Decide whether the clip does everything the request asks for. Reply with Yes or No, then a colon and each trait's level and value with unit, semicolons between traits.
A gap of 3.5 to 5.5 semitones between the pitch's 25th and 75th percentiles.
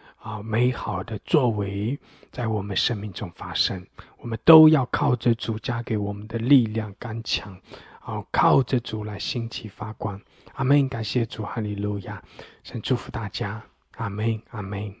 No: average, 2.9 semitones